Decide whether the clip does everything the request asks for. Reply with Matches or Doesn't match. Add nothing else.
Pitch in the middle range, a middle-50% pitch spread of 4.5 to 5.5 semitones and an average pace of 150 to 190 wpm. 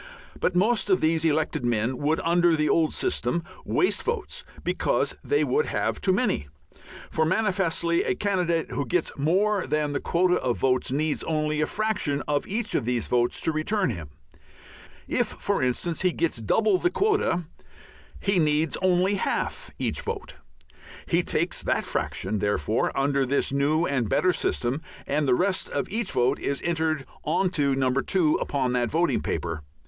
Matches